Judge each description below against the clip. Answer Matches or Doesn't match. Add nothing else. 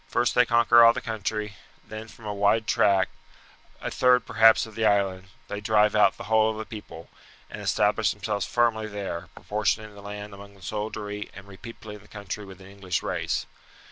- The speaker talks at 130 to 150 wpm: Doesn't match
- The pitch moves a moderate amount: Doesn't match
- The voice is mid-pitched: Doesn't match